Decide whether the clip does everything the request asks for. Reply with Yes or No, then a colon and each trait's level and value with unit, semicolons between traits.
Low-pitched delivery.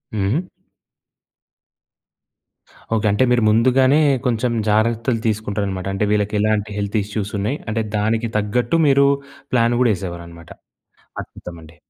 Yes: low, 110 Hz